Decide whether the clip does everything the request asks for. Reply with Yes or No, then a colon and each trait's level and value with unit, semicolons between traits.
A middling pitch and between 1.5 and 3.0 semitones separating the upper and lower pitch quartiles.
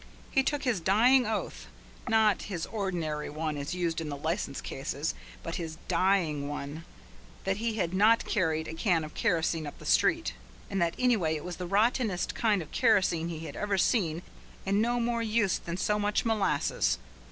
No: medium, 180 Hz; average, 5.0 semitones